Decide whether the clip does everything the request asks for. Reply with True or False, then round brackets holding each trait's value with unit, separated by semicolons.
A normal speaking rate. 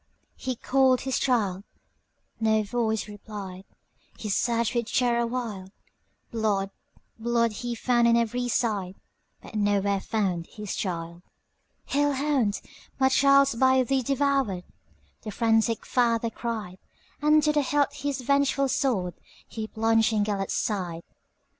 False (110 wpm)